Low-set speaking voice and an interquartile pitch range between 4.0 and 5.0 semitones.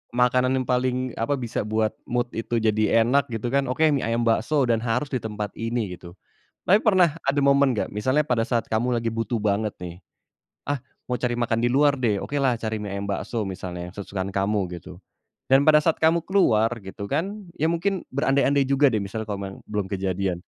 Yes: low, 120 Hz; average, 4.6 semitones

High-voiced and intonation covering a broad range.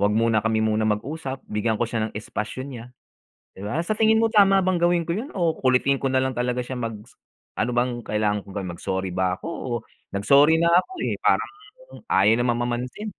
No: low, 125 Hz; wide, 6.8 semitones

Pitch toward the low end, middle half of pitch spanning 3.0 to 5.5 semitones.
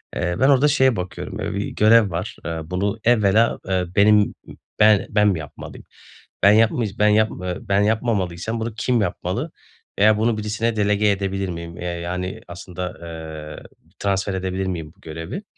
Yes: low, 100 Hz; average, 3.3 semitones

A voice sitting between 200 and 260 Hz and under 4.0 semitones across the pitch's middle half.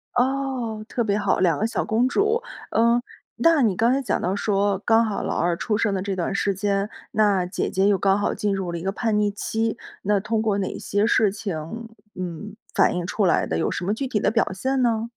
Yes: high, 210 Hz; average, 2.9 semitones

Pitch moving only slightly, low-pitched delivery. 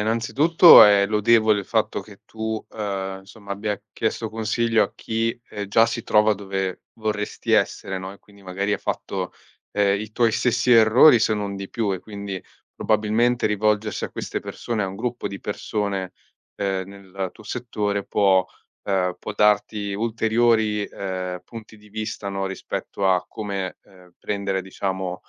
Yes: narrow, 2.2 semitones; low, 105 Hz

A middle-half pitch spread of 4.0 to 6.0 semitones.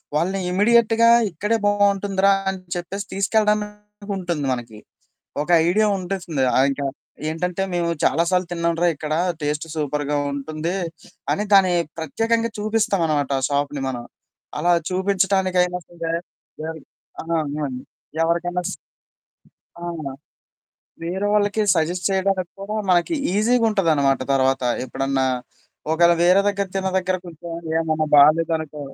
Yes: average, 4.4 semitones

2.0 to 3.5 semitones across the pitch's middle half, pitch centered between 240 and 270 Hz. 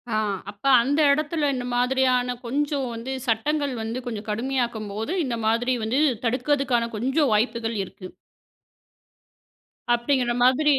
Yes: average, 3.2 semitones; very high, 250 Hz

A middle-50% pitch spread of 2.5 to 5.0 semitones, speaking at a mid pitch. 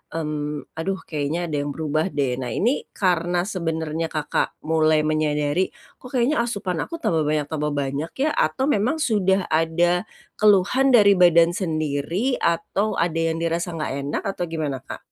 Yes: average, 4.0 semitones; medium, 165 Hz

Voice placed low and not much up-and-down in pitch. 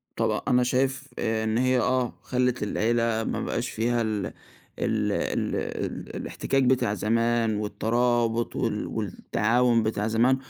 Yes: low, 115 Hz; narrow, 2.1 semitones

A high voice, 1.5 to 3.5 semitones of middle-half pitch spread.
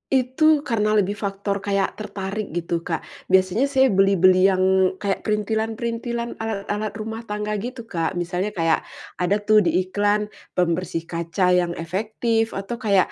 Yes: high, 205 Hz; average, 3.0 semitones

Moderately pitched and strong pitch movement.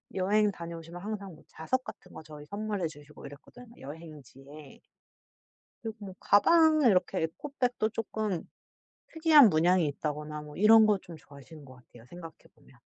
Yes: medium, 175 Hz; wide, 6.1 semitones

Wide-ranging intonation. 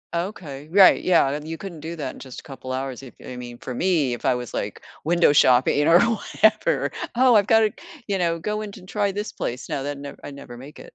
Yes: wide, 6.6 semitones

